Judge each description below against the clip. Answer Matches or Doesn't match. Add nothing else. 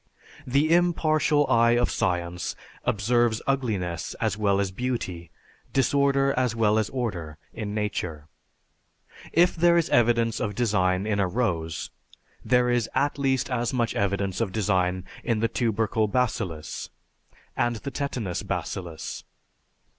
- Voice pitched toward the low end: Matches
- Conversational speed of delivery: Doesn't match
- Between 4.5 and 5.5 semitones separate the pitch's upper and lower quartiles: Matches